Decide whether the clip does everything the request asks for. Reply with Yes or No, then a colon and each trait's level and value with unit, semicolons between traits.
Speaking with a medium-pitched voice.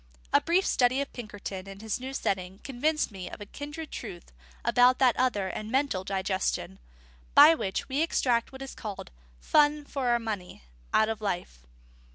No: high, 235 Hz